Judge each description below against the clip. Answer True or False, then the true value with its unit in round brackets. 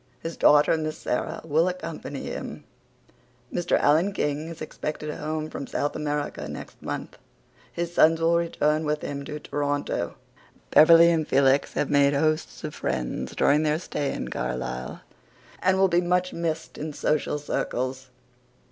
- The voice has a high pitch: False (150 Hz)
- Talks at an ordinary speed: True (150 wpm)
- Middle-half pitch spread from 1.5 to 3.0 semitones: True (2.4 semitones)